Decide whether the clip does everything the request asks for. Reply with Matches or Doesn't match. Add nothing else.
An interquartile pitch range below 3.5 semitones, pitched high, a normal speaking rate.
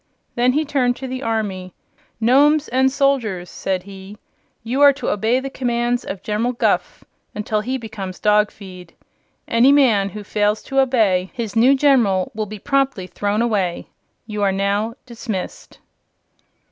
Doesn't match